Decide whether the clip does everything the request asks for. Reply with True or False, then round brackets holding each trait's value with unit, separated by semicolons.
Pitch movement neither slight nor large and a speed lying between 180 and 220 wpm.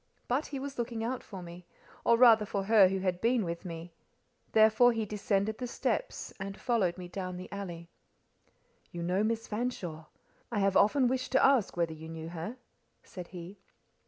True (4.7 semitones; 185 wpm)